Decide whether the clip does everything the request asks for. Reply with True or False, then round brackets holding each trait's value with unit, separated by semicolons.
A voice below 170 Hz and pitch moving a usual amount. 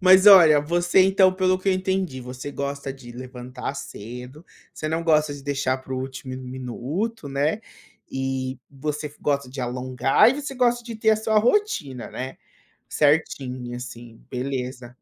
False (140 Hz; 6.3 semitones)